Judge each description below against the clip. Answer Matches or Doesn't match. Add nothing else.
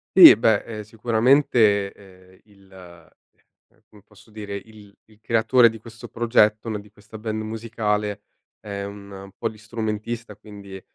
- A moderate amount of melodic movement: Doesn't match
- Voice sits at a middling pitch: Doesn't match